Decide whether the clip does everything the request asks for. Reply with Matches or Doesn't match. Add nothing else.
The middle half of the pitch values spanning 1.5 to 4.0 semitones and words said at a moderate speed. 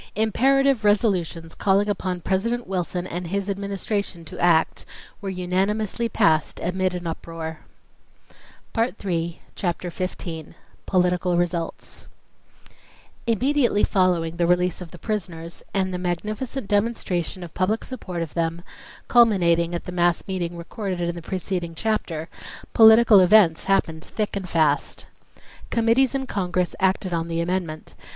Doesn't match